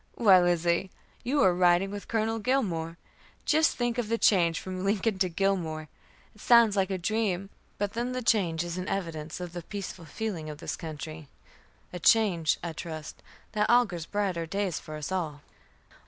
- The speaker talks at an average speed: Yes, average, 175 wpm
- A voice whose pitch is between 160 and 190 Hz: Yes, medium, 185 Hz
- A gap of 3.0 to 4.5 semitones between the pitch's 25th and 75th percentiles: Yes, average, 4.2 semitones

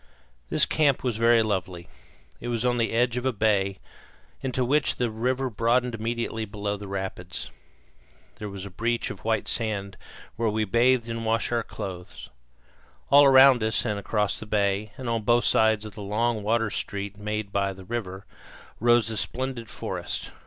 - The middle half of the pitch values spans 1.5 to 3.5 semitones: Yes, average, 2.8 semitones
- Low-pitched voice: Yes, low, 110 Hz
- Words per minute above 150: Yes, average, 175 wpm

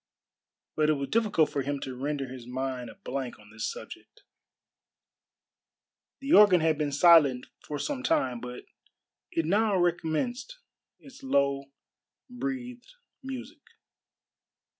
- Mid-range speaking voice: Yes, medium, 160 Hz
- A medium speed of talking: No, slow, 125 wpm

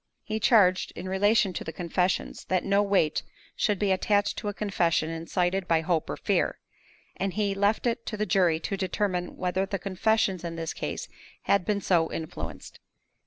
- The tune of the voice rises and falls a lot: No, narrow, 2.6 semitones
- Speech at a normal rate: Yes, average, 180 wpm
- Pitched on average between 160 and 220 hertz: Yes, high, 190 Hz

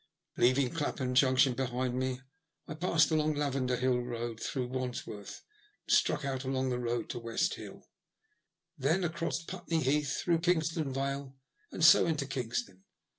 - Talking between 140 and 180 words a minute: Yes, average, 155 wpm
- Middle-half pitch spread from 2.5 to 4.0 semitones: Yes, average, 3.6 semitones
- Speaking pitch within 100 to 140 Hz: Yes, low, 135 Hz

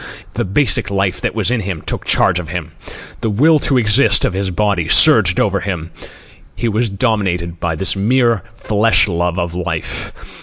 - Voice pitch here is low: Yes, low, 100 Hz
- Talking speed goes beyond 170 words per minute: Yes, average, 180 wpm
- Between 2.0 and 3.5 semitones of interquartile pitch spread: No, average, 4.1 semitones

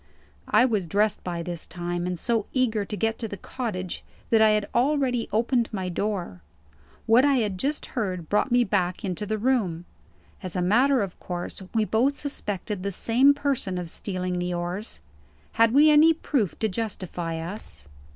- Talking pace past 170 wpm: Yes, average, 180 wpm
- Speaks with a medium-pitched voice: No, high, 210 Hz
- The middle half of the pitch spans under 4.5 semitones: No, average, 4.8 semitones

